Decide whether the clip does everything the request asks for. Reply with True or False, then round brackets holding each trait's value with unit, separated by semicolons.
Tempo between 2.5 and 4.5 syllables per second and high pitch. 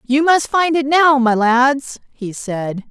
True (3.4 syllables/s; 265 Hz)